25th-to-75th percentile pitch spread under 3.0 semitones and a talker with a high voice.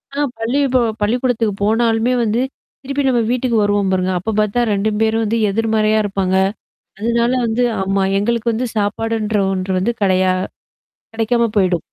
Yes: narrow, 2.6 semitones; high, 220 Hz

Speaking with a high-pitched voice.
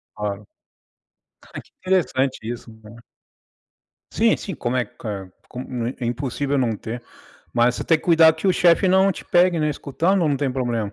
No: low, 130 Hz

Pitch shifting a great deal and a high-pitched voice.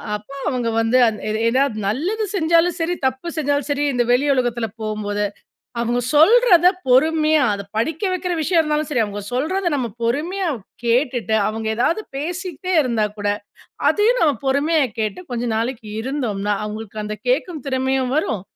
Yes: wide, 6.3 semitones; very high, 265 Hz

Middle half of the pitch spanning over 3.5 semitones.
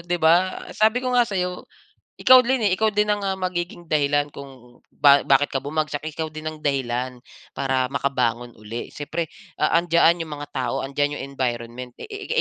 Yes: average, 4.9 semitones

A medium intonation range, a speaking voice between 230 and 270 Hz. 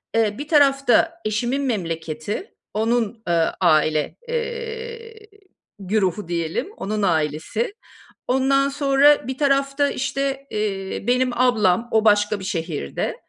No: wide, 6.3 semitones; high, 235 Hz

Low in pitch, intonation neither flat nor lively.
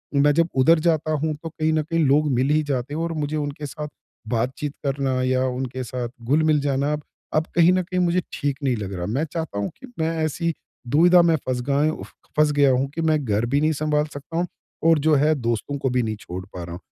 No: medium, 145 Hz; average, 3.5 semitones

